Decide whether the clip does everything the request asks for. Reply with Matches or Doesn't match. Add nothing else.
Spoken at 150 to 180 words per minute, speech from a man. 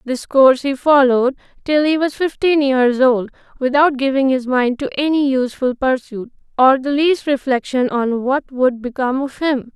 Doesn't match